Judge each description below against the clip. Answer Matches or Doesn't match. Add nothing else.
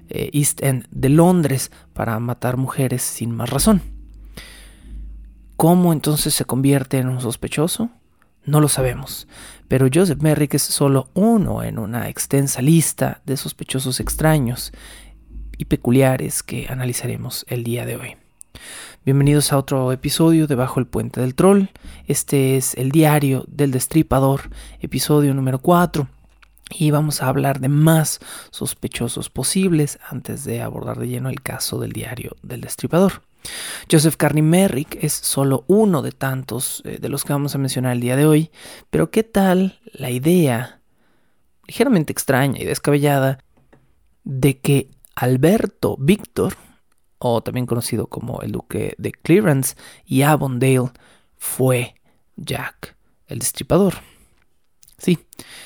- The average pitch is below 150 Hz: Matches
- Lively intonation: Doesn't match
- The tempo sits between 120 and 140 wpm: Matches